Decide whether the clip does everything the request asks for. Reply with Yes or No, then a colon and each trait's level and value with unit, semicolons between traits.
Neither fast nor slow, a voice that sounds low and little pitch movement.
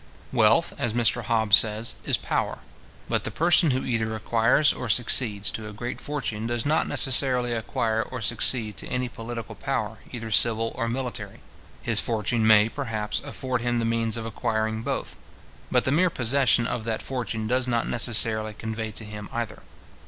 Yes: average, 175 wpm; low, 115 Hz; narrow, 2.1 semitones